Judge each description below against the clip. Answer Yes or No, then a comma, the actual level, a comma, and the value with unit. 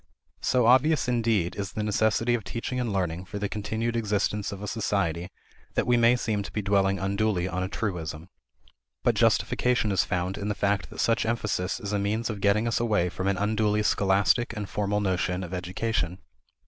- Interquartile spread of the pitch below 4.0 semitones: Yes, average, 2.9 semitones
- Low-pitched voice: Yes, low, 105 Hz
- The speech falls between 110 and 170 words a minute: No, average, 195 wpm